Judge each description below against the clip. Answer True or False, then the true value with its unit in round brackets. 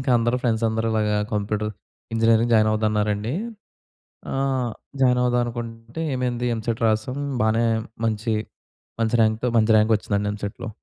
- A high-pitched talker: False (115 Hz)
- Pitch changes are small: True (1.8 semitones)